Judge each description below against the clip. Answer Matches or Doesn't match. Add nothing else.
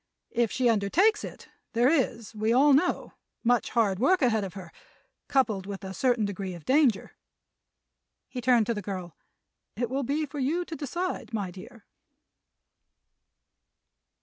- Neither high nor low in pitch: Doesn't match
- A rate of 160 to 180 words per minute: Doesn't match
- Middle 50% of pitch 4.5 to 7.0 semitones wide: Matches